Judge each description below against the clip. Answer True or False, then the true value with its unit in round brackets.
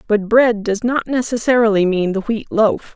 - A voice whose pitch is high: True (220 Hz)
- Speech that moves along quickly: False (185 wpm)